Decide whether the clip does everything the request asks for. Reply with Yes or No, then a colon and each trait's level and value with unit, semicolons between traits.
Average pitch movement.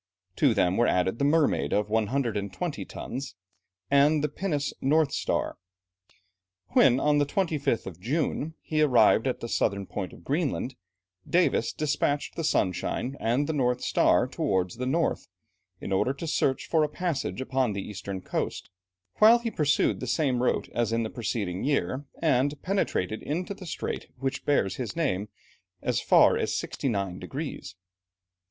No: wide, 5.8 semitones